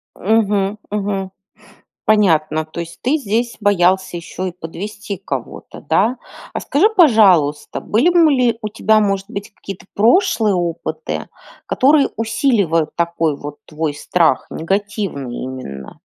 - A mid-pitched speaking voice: No, high, 195 Hz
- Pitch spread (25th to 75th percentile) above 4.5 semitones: Yes, average, 5.2 semitones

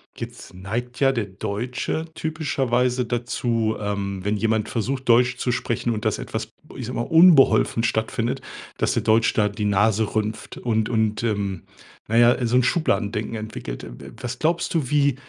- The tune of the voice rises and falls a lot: No, average, 2.9 semitones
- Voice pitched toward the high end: No, low, 115 Hz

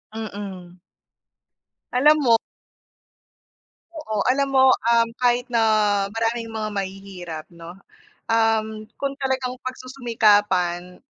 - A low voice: No, high, 225 Hz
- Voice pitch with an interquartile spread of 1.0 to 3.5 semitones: No, average, 4.3 semitones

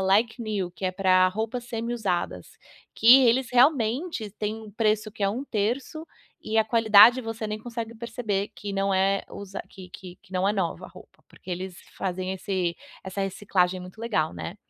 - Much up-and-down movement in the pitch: No, average, 3.3 semitones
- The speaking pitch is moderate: No, high, 210 Hz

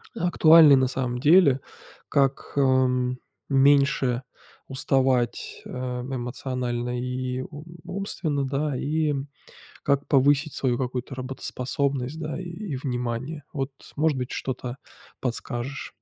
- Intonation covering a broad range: No, narrow, 2.4 semitones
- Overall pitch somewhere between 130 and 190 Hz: Yes, low, 135 Hz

